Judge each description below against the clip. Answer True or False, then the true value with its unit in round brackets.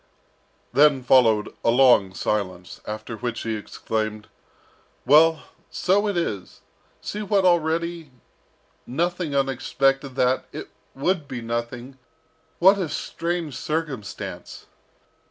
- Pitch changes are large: True (6.2 semitones)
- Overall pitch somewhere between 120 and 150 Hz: True (135 Hz)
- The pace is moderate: False (105 wpm)